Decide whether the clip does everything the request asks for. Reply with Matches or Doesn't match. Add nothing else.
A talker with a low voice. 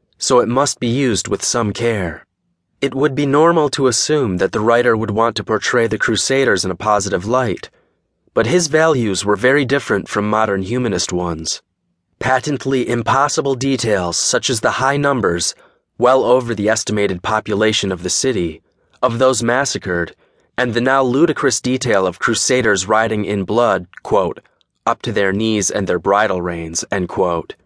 Matches